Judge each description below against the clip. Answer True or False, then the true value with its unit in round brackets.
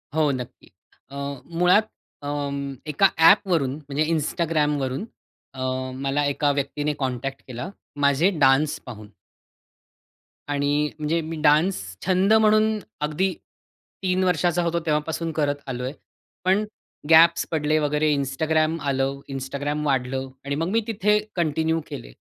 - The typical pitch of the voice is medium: True (150 Hz)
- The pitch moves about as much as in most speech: True (3.3 semitones)